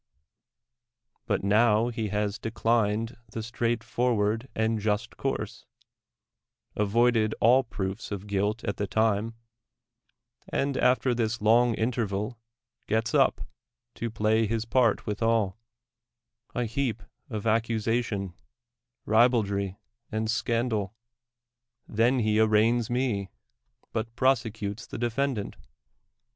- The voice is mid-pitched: No, low, 110 Hz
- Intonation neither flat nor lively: No, narrow, 2.1 semitones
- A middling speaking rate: No, slow, 105 wpm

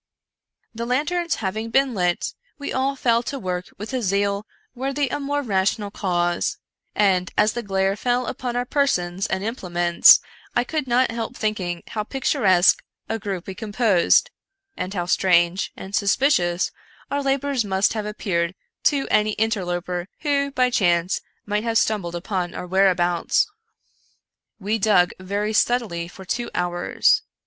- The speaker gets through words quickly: No, average, 155 wpm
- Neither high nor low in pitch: No, high, 210 Hz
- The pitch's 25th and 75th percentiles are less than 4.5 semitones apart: No, average, 5.1 semitones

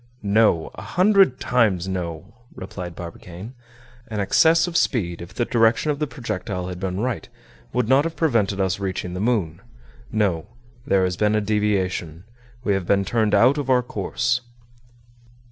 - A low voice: Yes, low, 105 Hz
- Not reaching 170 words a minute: Yes, average, 160 wpm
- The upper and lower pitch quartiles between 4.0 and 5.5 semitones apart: Yes, average, 5.2 semitones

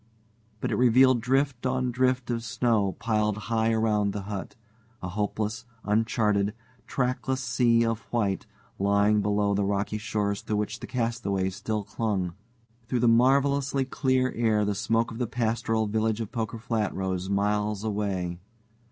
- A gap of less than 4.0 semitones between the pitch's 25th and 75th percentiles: Yes, average, 2.8 semitones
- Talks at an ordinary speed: Yes, average, 150 wpm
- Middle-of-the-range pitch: No, low, 110 Hz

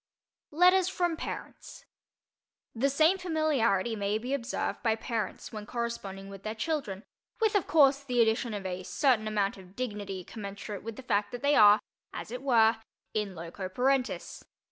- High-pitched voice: Yes, high, 230 Hz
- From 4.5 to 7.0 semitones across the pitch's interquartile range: Yes, wide, 5.4 semitones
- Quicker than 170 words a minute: No, average, 165 wpm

